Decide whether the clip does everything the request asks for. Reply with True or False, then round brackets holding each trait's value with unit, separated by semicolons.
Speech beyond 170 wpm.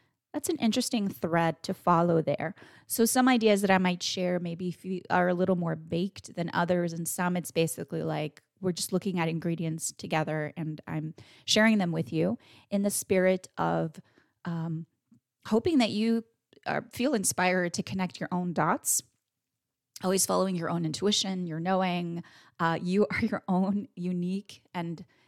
False (165 wpm)